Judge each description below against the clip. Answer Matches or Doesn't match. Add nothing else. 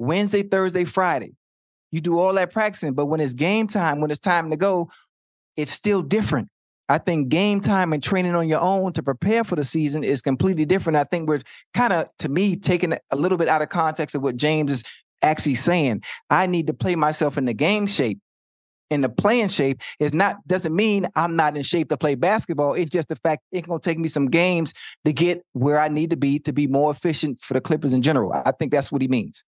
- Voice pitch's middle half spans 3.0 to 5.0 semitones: Matches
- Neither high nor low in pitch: Matches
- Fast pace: Matches